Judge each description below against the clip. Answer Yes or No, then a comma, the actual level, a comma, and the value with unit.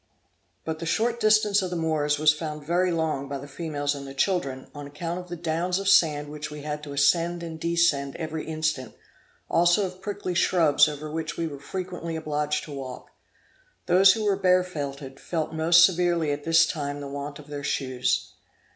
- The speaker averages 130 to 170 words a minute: No, average, 190 wpm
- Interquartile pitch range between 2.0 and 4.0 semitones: Yes, average, 3.2 semitones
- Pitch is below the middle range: No, medium, 160 Hz